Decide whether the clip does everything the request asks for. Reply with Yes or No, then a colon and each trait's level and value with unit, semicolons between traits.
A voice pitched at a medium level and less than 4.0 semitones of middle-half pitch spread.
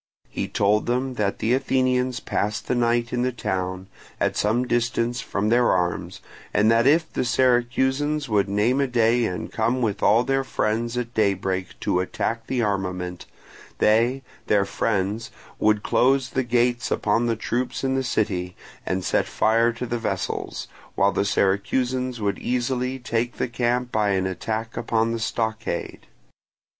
No: low, 115 Hz; average, 3.2 semitones